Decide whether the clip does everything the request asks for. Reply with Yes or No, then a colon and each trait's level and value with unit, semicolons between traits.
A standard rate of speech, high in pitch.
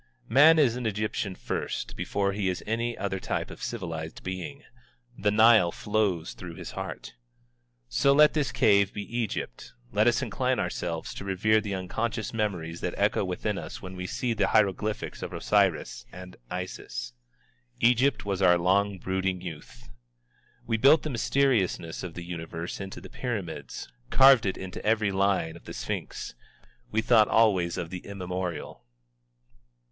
No: average, 155 wpm; low, 100 Hz